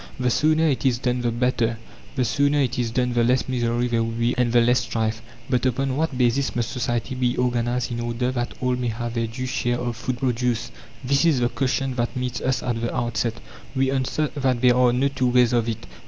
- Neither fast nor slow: No, fast, 230 wpm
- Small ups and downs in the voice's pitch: Yes, narrow, 1.5 semitones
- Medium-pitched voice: No, low, 125 Hz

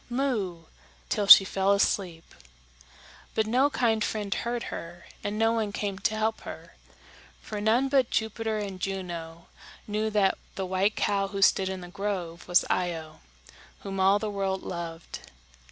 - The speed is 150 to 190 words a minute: Yes, average, 155 wpm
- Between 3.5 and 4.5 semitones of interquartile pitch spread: No, average, 2.8 semitones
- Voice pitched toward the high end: Yes, high, 200 Hz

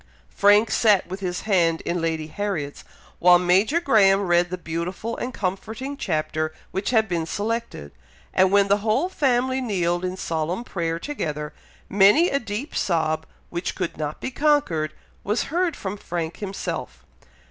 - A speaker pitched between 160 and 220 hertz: Yes, high, 190 Hz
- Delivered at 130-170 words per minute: Yes, average, 155 wpm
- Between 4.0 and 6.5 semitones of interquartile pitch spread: Yes, average, 4.8 semitones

